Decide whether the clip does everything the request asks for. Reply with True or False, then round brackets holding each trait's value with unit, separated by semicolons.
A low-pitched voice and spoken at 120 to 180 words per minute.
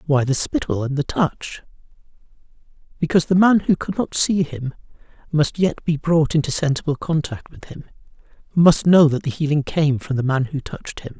False (155 Hz; 175 wpm)